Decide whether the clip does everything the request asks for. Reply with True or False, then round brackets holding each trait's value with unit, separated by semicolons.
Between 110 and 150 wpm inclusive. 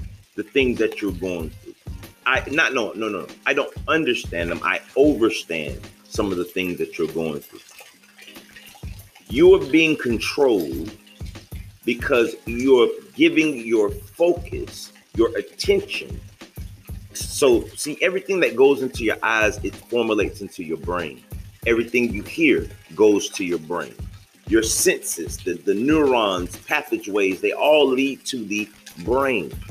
True (140 wpm)